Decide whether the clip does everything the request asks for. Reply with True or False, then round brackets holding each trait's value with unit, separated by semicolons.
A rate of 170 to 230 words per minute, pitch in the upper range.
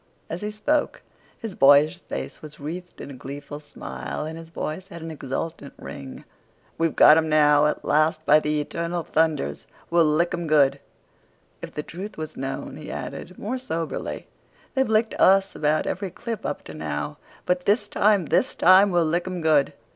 False (175 wpm; 160 Hz)